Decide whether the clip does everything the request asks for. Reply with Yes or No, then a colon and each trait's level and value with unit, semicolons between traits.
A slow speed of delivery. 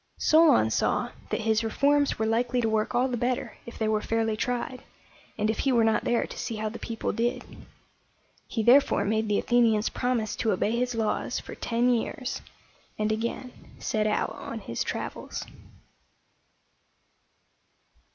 No: average, 160 wpm